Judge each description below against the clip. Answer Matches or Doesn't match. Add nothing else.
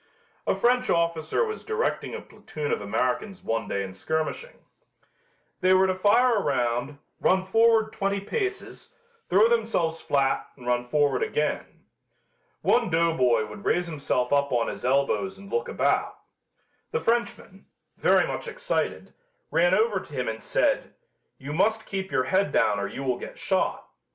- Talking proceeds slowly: Doesn't match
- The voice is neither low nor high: Matches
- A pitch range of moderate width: Doesn't match